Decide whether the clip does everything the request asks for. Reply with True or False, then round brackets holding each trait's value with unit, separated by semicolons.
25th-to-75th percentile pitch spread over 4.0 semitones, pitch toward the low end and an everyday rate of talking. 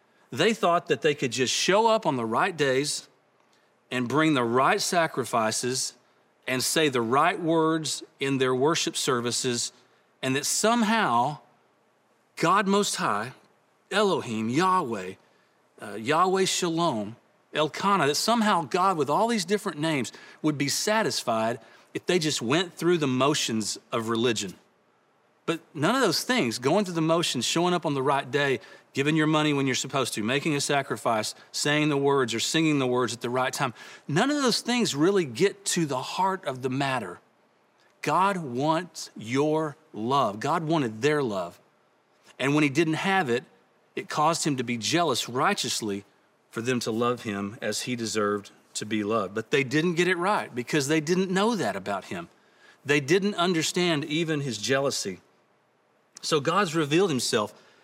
False (5.6 semitones; 145 Hz; 165 wpm)